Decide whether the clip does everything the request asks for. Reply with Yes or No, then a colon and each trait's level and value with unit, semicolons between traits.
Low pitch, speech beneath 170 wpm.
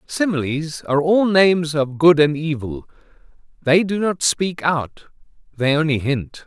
No: medium, 155 Hz; average, 150 wpm